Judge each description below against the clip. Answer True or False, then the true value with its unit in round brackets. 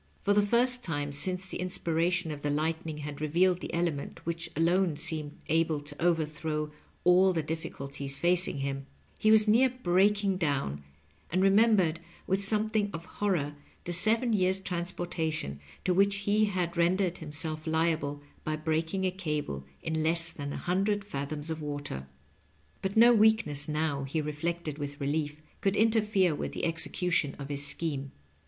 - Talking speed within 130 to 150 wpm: False (160 wpm)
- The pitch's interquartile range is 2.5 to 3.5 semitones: False (4.1 semitones)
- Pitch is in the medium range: True (165 Hz)